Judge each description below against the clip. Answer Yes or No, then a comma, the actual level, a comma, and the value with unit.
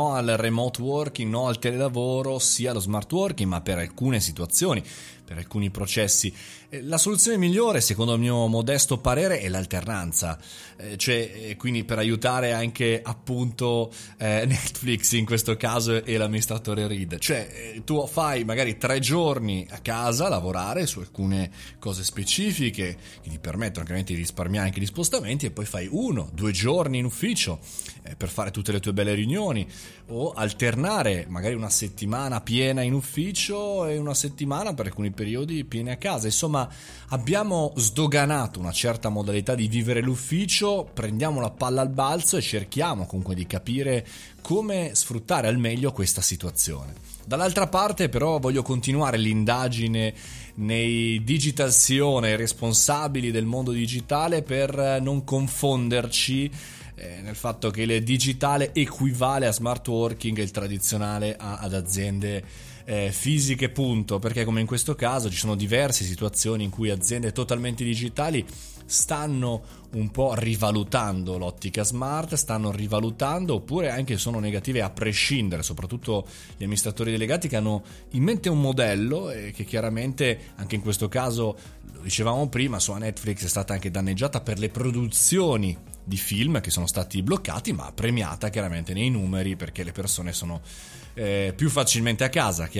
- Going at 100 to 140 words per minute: No, average, 150 wpm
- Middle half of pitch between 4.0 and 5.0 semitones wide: Yes, average, 4.5 semitones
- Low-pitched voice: Yes, low, 115 Hz